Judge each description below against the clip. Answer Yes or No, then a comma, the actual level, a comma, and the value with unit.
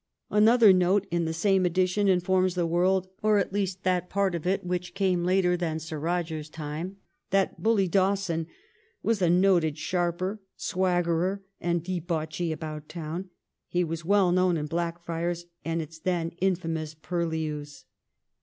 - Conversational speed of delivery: Yes, average, 150 wpm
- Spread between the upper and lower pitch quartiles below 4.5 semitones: Yes, narrow, 2.4 semitones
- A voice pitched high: No, medium, 175 Hz